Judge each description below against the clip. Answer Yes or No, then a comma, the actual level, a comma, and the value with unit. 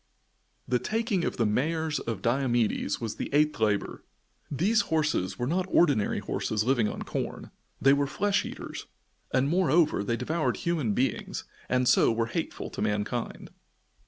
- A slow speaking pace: No, average, 155 wpm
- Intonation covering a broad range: Yes, wide, 5.7 semitones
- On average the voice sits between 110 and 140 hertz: Yes, low, 135 Hz